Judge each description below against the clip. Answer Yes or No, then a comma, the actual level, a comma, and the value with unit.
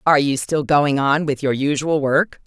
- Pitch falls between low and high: Yes, medium, 145 Hz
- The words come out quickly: Yes, fast, 220 wpm